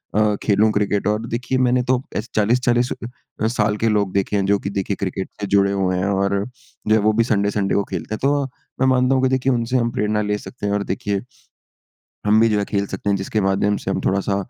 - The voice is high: No, low, 105 Hz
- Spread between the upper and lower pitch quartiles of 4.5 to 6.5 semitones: No, average, 2.8 semitones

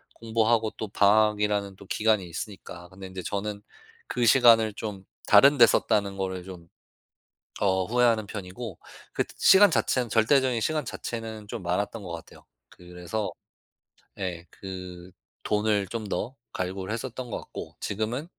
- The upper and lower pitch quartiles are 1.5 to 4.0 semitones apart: Yes, average, 3.2 semitones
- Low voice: Yes, low, 105 Hz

